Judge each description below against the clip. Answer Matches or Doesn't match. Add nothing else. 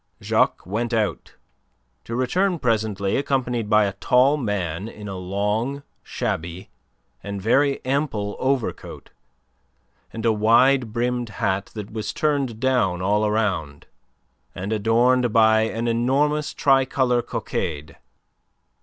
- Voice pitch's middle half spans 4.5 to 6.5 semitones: Doesn't match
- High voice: Doesn't match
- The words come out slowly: Matches